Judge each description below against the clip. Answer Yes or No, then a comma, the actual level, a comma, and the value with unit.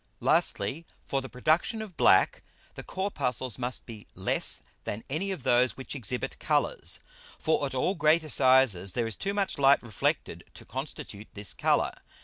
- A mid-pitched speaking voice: No, low, 130 Hz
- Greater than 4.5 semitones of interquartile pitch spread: Yes, average, 5.1 semitones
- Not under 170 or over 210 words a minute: No, average, 160 wpm